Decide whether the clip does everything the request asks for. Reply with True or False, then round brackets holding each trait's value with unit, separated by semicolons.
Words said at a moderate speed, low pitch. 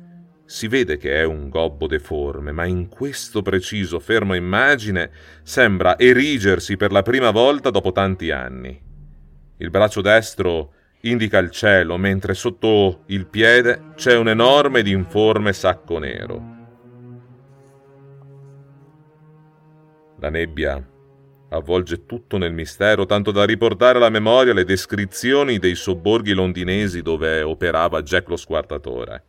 True (125 wpm; 105 Hz)